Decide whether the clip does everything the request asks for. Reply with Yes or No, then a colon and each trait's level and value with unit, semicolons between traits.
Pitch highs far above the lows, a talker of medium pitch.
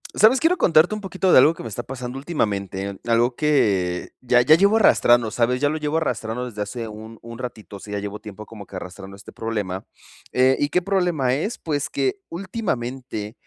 No: wide, 6.7 semitones; low, 125 Hz